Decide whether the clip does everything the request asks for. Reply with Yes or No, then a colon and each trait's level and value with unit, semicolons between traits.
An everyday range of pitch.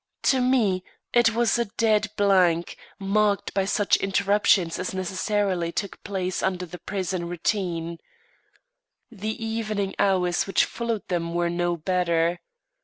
Yes: average, 3.2 semitones